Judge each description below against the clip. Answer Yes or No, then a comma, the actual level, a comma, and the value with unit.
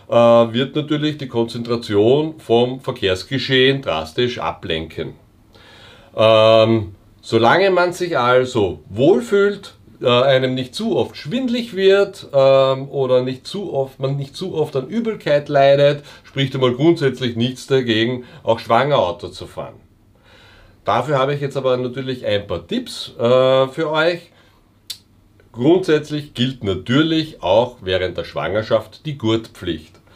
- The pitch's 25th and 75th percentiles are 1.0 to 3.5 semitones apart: No, average, 4.7 semitones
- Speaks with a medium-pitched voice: No, low, 130 Hz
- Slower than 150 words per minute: Yes, slow, 125 wpm